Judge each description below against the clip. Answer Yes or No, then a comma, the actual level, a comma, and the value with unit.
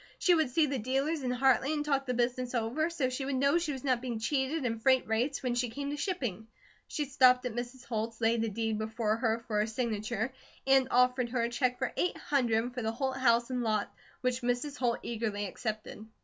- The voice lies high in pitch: Yes, very high, 250 Hz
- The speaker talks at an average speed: No, fast, 225 wpm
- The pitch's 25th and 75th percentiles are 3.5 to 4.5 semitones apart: No, average, 2.8 semitones